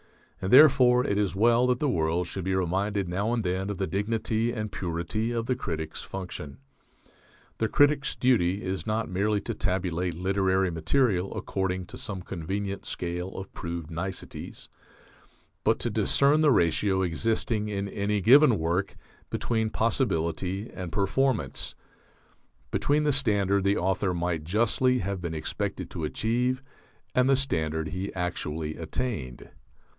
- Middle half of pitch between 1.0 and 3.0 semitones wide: No, average, 4.5 semitones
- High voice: No, low, 100 Hz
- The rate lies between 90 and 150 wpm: Yes, average, 145 wpm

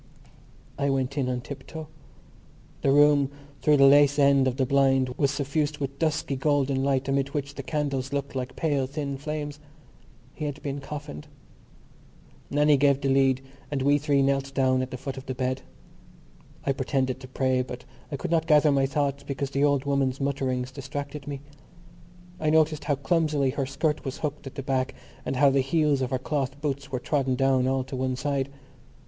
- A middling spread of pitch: No, narrow, 1.6 semitones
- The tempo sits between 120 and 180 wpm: No, average, 190 wpm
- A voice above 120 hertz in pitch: Yes, medium, 140 Hz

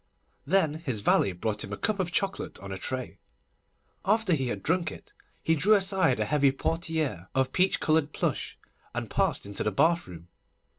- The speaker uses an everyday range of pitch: No, wide, 8.9 semitones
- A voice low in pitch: No, medium, 150 Hz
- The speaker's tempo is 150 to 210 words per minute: Yes, average, 180 wpm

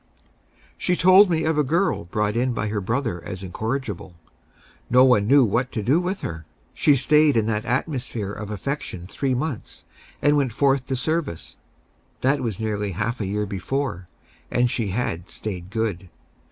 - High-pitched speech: No, low, 120 Hz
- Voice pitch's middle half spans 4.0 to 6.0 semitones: Yes, average, 5.3 semitones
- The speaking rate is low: No, average, 170 wpm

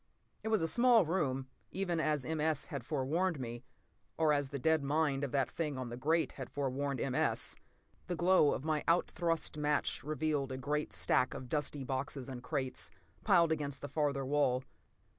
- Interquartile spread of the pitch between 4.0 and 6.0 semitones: No, average, 3.2 semitones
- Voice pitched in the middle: Yes, medium, 145 Hz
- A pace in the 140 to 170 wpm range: No, average, 190 wpm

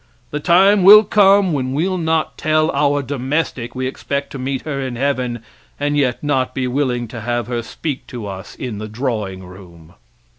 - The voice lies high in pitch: No, low, 135 Hz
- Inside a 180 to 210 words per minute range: Yes, average, 185 wpm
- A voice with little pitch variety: No, average, 4.0 semitones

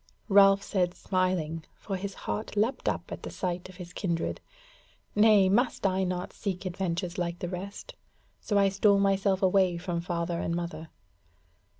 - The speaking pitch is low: No, medium, 185 Hz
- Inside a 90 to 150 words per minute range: No, average, 165 wpm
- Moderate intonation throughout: No, narrow, 2.2 semitones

